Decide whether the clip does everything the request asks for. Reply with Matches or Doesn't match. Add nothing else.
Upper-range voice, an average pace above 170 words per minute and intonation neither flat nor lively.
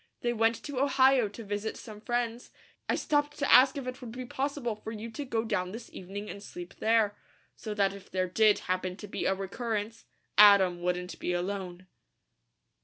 Matches